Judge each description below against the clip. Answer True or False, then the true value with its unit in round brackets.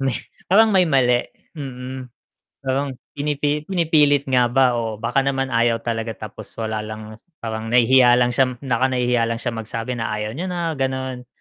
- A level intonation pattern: False (3.0 semitones)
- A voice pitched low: True (125 Hz)